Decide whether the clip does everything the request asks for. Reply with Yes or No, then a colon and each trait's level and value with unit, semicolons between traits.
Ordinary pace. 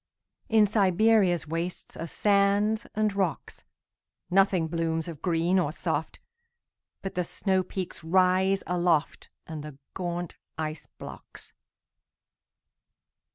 No: slow, 85 wpm